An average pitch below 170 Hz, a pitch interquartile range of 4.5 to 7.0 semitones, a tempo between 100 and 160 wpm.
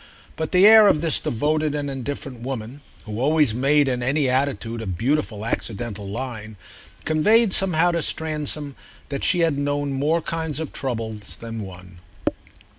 Yes: medium, 140 Hz; average, 5.1 semitones; average, 155 wpm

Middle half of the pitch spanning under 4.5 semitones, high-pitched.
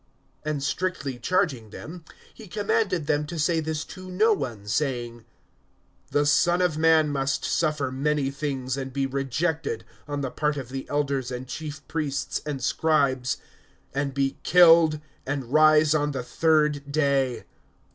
No: average, 2.8 semitones; medium, 145 Hz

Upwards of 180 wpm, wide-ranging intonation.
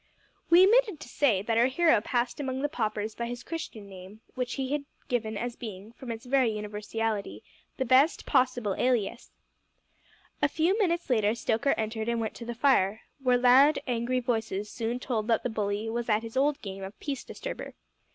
No: average, 190 wpm; average, 3.3 semitones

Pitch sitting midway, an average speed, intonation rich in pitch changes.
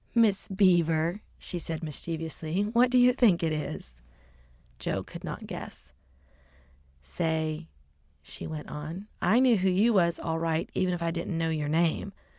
No: medium, 170 Hz; average, 160 wpm; average, 3.5 semitones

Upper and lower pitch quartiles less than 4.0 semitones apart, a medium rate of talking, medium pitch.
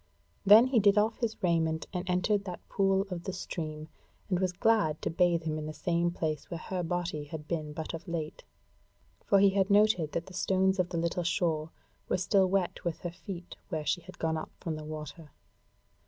No: average, 3.1 semitones; fast, 210 wpm; medium, 175 Hz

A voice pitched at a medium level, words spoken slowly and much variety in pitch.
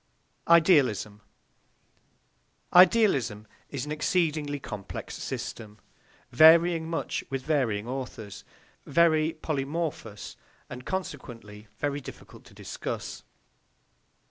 Yes: medium, 145 Hz; slow, 85 wpm; wide, 6.1 semitones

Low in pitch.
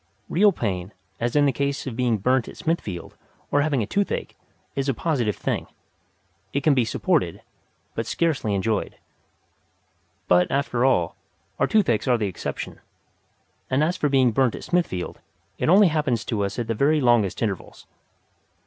Yes: low, 125 Hz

